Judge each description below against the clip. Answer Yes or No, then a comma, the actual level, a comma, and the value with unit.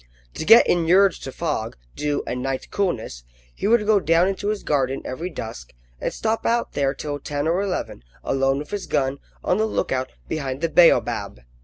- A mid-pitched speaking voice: Yes, medium, 155 Hz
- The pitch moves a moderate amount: No, wide, 6.3 semitones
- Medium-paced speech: Yes, average, 185 wpm